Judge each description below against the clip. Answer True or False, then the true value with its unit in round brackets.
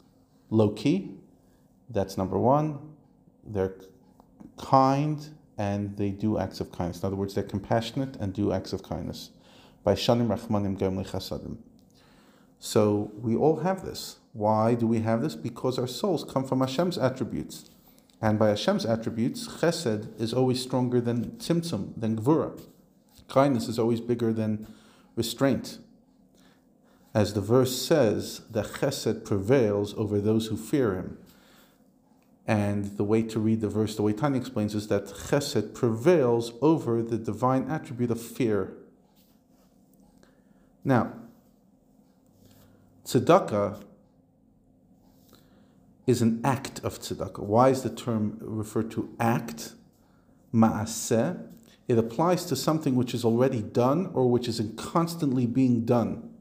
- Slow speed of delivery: True (130 wpm)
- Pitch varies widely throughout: False (3.6 semitones)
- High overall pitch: False (115 Hz)